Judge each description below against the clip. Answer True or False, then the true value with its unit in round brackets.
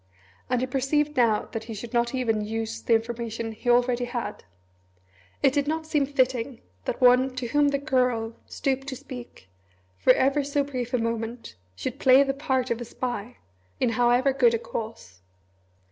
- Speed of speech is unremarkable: True (175 wpm)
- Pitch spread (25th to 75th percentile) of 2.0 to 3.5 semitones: True (2.8 semitones)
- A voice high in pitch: True (250 Hz)